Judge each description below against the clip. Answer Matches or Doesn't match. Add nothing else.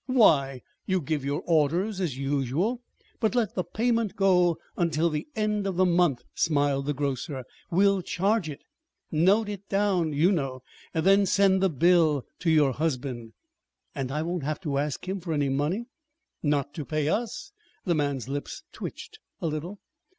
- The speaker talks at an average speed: Matches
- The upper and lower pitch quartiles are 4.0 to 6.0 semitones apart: Matches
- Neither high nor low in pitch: Matches